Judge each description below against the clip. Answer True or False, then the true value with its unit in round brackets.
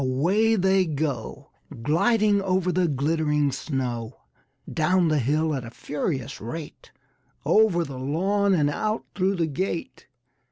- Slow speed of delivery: True (130 wpm)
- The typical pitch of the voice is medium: True (160 Hz)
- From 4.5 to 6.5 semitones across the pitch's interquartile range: True (5.2 semitones)